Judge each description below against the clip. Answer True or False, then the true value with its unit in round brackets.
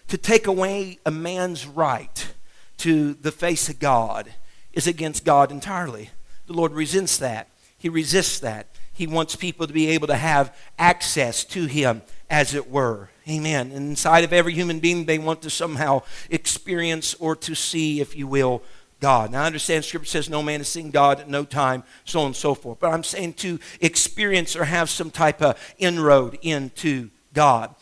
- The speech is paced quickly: False (185 wpm)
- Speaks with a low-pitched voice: False (155 Hz)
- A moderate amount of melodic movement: True (3.1 semitones)